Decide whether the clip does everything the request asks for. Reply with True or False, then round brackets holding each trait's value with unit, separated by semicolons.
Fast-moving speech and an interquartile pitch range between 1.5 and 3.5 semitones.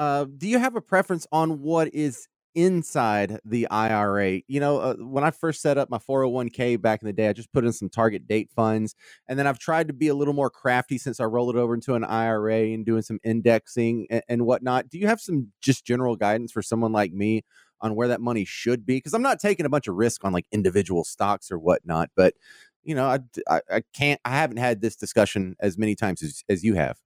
False (240 wpm; 4.6 semitones)